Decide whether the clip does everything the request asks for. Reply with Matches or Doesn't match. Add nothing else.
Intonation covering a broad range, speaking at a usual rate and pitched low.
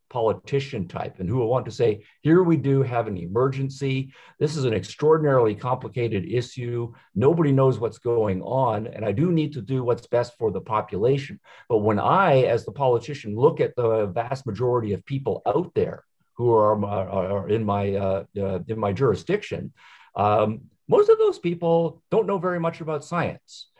Matches